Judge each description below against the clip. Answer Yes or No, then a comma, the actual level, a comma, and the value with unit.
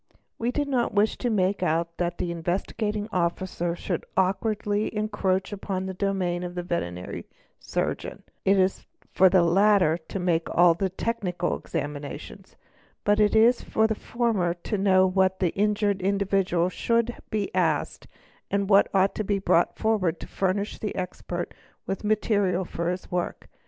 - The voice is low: No, high, 190 Hz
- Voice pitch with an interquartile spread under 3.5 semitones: Yes, average, 2.8 semitones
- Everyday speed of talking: Yes, average, 160 wpm